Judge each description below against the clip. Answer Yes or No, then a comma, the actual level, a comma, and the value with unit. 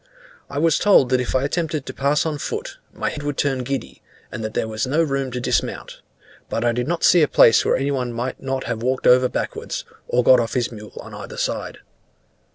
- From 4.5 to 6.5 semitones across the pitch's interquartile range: No, average, 2.8 semitones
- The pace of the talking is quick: Yes, fast, 230 wpm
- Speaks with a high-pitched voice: No, low, 130 Hz